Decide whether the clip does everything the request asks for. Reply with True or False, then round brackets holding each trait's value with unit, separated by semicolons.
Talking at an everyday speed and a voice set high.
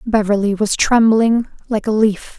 True (150 wpm; 215 Hz)